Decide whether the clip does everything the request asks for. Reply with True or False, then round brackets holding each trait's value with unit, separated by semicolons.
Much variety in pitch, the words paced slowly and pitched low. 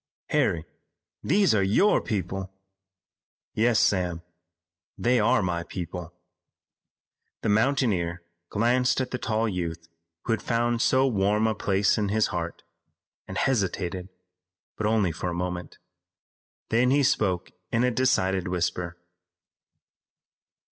False (4.9 semitones; 120 wpm; 105 Hz)